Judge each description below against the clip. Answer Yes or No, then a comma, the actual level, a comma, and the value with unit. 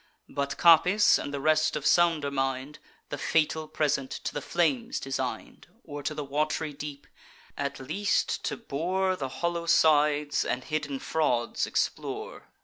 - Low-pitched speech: No, medium, 150 Hz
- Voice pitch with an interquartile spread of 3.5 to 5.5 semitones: No, average, 2.8 semitones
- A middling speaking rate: Yes, average, 145 wpm